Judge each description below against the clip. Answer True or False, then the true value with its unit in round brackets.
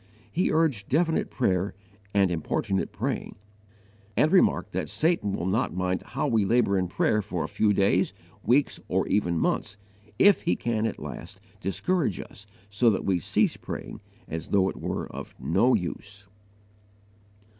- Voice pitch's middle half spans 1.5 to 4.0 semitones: False (5.0 semitones)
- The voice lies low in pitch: True (100 Hz)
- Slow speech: False (155 wpm)